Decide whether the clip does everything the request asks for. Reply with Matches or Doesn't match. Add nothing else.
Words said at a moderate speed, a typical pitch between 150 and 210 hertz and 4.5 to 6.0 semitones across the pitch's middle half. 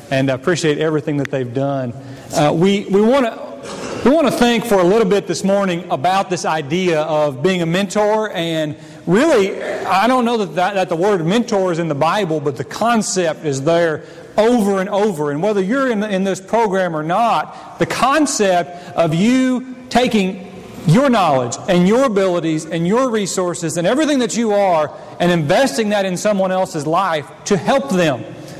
Matches